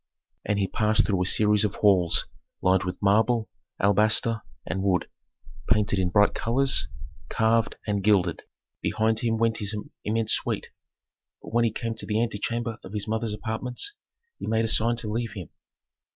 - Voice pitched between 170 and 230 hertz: No, low, 110 Hz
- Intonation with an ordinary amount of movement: No, narrow, 2.0 semitones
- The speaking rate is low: No, average, 165 wpm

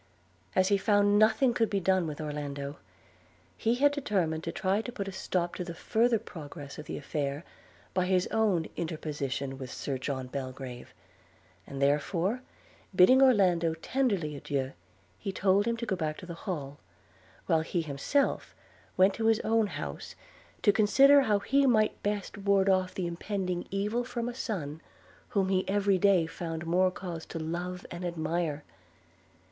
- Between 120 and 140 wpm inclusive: No, average, 165 wpm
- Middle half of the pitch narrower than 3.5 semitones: No, average, 4.7 semitones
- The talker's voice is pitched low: No, medium, 185 Hz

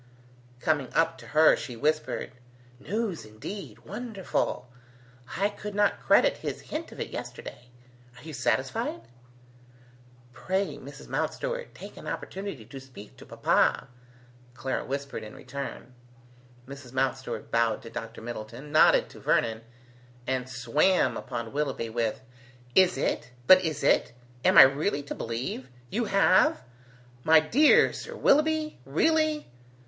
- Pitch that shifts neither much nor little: No, wide, 7.7 semitones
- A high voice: No, medium, 140 Hz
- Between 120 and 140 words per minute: Yes, slow, 135 wpm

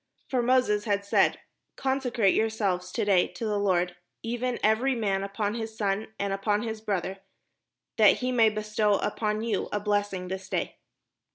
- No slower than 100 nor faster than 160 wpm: No, average, 170 wpm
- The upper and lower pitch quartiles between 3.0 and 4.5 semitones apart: No, narrow, 2.4 semitones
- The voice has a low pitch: No, high, 210 Hz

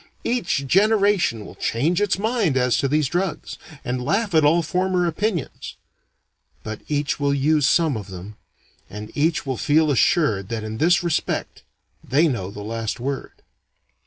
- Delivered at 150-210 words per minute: Yes, average, 160 wpm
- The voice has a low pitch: No, medium, 145 Hz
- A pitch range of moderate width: No, wide, 6.8 semitones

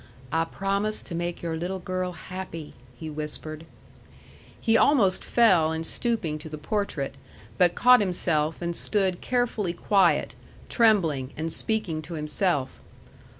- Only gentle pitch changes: No, average, 4.1 semitones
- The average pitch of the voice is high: No, medium, 175 Hz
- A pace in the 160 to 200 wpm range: No, slow, 135 wpm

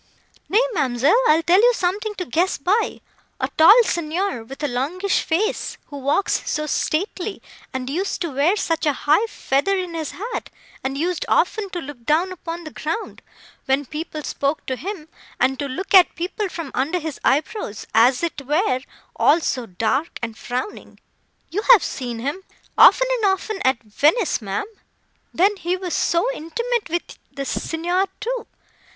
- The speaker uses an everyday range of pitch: No, wide, 5.7 semitones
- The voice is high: Yes, very high, 330 Hz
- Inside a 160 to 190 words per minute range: Yes, average, 165 wpm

